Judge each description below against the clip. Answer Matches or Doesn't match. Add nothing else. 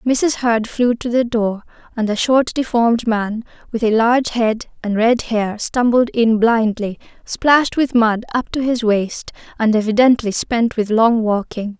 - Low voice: Doesn't match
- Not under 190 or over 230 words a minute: Doesn't match